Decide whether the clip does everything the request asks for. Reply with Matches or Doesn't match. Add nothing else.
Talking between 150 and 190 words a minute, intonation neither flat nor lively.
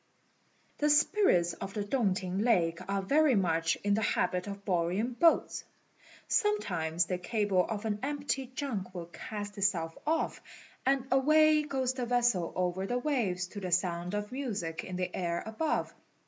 Doesn't match